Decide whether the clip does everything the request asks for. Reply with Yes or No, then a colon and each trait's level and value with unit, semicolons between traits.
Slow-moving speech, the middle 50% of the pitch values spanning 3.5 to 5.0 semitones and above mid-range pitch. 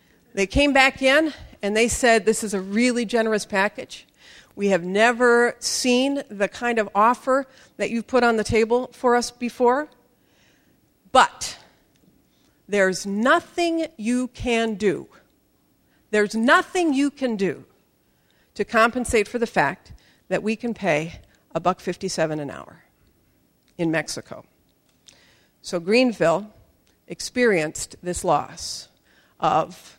Yes: slow, 125 wpm; average, 4.0 semitones; high, 230 Hz